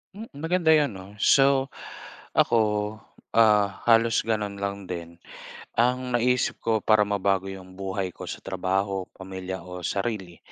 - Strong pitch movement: No, average, 3.7 semitones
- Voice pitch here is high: No, low, 100 Hz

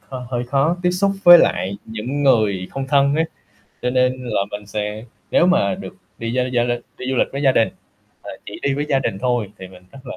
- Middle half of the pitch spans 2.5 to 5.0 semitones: Yes, average, 4.3 semitones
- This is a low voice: Yes, low, 125 Hz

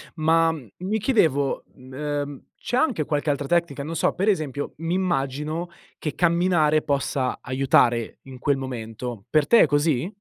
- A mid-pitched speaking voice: Yes, medium, 150 Hz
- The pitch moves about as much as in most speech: Yes, average, 3.9 semitones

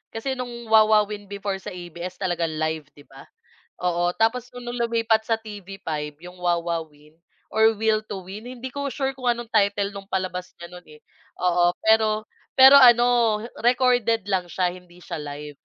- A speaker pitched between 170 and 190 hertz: No, high, 205 Hz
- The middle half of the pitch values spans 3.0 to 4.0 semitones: No, average, 4.8 semitones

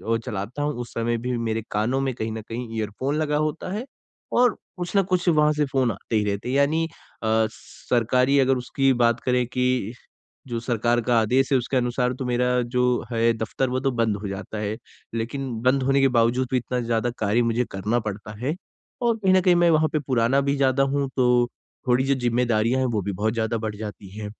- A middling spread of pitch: Yes, average, 3.3 semitones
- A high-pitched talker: No, low, 125 Hz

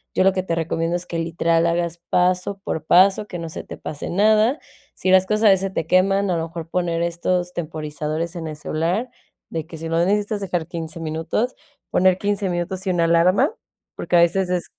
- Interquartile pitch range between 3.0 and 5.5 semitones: No, narrow, 2.4 semitones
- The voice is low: No, medium, 175 Hz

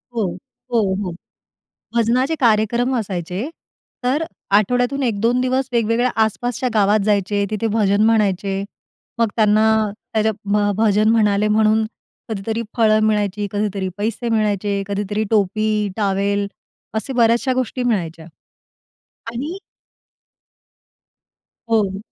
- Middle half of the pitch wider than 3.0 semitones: No, narrow, 2.5 semitones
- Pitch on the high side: Yes, high, 215 Hz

